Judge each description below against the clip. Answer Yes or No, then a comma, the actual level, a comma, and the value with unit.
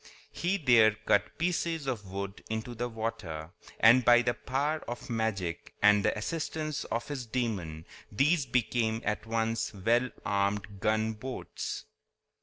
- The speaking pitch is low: Yes, low, 115 Hz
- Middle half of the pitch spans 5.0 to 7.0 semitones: No, average, 3.7 semitones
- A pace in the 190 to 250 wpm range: No, slow, 135 wpm